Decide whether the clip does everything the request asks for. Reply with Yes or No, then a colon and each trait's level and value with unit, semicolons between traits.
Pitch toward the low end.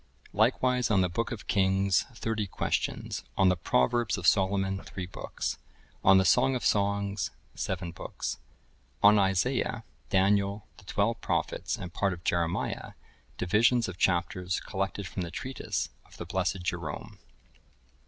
Yes: very low, 95 Hz